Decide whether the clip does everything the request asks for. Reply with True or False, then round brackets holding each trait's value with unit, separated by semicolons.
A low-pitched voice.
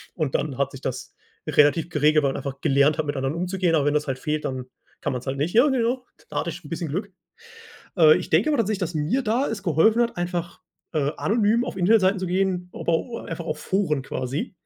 False (165 Hz)